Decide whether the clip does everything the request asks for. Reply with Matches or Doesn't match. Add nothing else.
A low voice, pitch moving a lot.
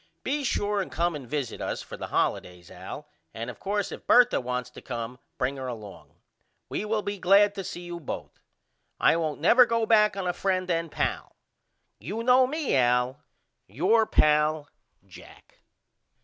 Doesn't match